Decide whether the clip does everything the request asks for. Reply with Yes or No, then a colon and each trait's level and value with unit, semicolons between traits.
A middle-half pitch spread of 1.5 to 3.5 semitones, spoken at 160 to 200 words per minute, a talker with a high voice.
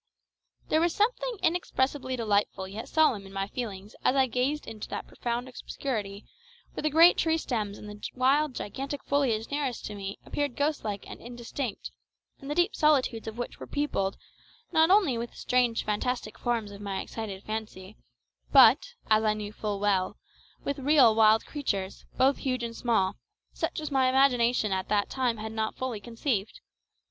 No: average, 4.8 semitones; average, 175 wpm; high, 240 Hz